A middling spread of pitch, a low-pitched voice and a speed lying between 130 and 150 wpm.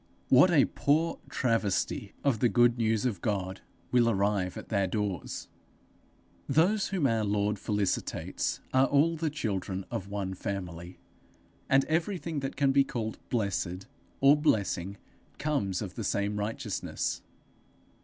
No: wide, 5.8 semitones; low, 110 Hz; slow, 135 wpm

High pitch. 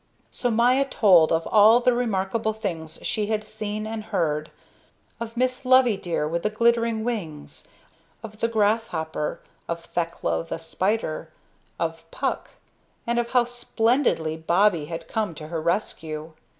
Yes: high, 210 Hz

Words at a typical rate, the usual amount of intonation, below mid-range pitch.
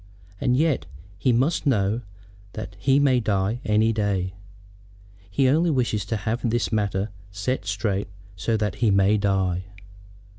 Yes: average, 145 wpm; average, 4.1 semitones; low, 110 Hz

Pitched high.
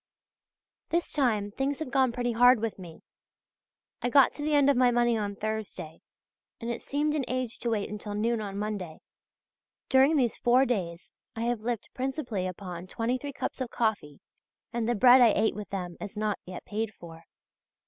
Yes: high, 230 Hz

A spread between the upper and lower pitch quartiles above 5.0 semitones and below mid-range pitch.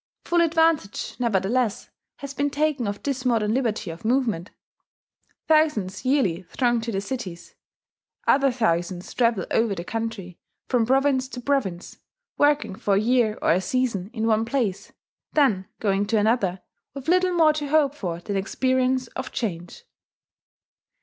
No: wide, 5.6 semitones; high, 235 Hz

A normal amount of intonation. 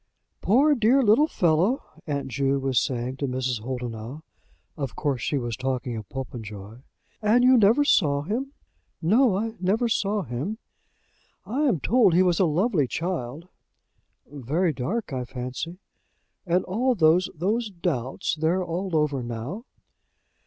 No: wide, 8.3 semitones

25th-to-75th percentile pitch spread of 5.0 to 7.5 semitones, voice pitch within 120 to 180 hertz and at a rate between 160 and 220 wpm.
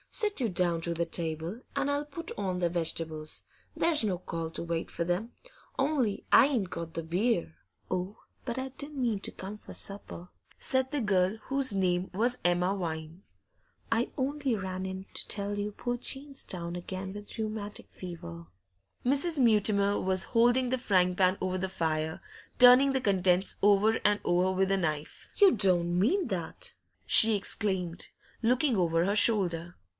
No: wide, 5.5 semitones; high, 195 Hz; average, 170 wpm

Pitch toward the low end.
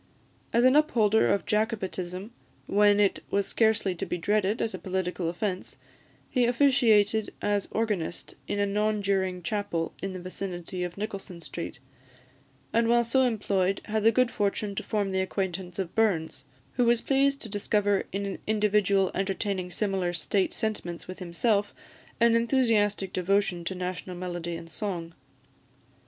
No: high, 200 Hz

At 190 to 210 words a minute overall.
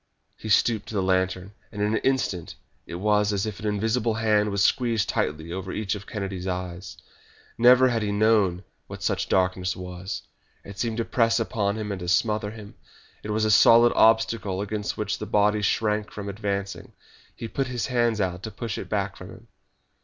Yes: average, 195 wpm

